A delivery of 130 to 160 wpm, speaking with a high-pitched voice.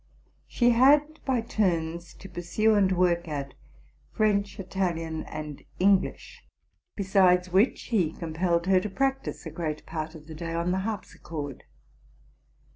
No: average, 140 wpm; medium, 180 Hz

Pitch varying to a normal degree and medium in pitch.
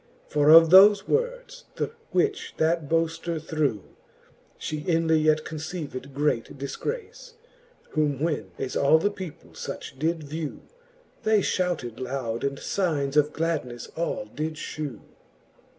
Yes: average, 3.3 semitones; medium, 155 Hz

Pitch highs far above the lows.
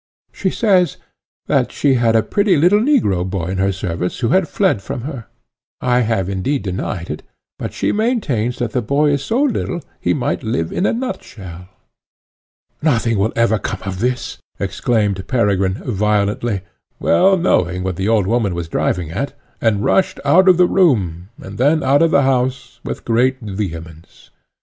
Yes: wide, 7.0 semitones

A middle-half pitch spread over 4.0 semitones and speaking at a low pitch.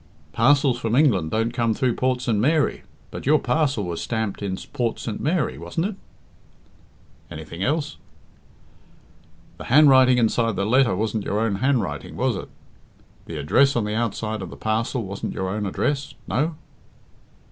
Yes: average, 4.6 semitones; low, 115 Hz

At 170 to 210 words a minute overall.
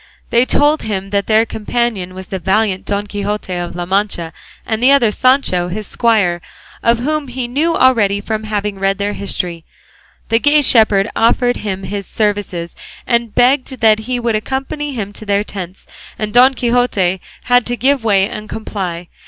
Yes: average, 175 wpm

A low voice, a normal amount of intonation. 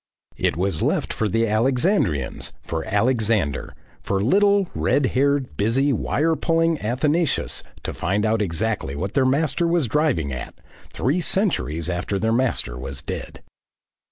No: low, 115 Hz; wide, 7.9 semitones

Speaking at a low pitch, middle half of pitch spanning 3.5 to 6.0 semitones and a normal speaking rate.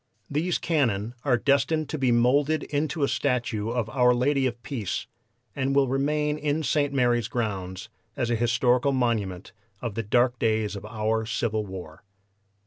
Yes: low, 125 Hz; average, 4.3 semitones; average, 160 wpm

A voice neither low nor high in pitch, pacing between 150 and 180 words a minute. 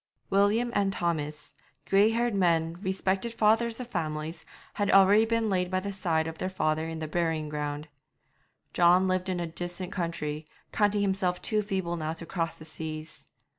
Yes: medium, 180 Hz; average, 170 wpm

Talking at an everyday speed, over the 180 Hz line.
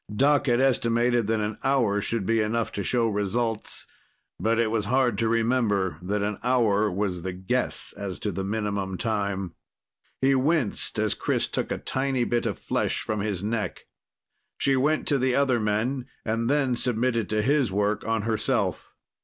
No: average, 175 wpm; low, 115 Hz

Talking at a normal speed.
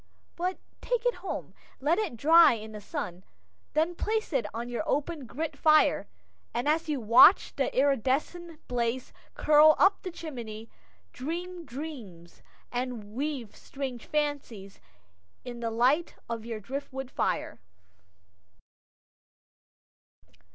No: slow, 125 wpm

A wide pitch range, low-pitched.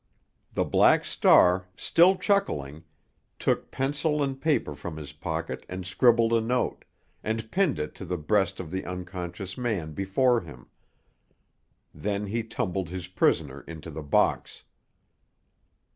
Yes: wide, 6.3 semitones; very low, 95 Hz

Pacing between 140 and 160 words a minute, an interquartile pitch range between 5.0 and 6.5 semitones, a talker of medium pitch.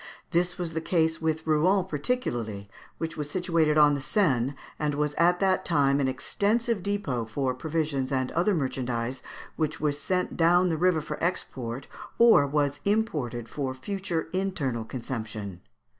Yes: average, 155 wpm; average, 5.3 semitones; medium, 150 Hz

